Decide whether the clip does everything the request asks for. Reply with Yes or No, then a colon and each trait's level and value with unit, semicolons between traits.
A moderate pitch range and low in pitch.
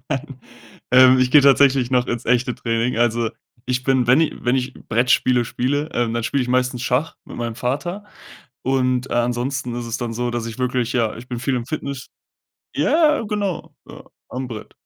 No: narrow, 2.0 semitones; low, 125 Hz